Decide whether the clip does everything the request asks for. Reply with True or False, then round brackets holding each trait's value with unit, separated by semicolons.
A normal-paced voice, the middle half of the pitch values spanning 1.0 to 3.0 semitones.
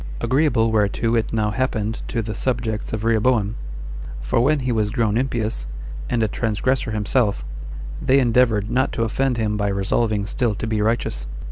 True (165 wpm; 2.6 semitones)